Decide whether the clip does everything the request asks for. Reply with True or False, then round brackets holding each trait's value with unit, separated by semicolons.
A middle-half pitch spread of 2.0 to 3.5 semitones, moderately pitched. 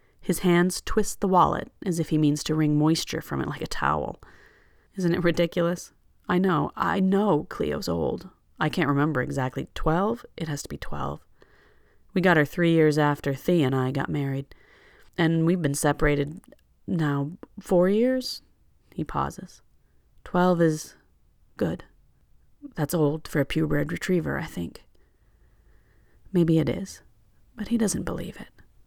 False (4.0 semitones; 165 Hz)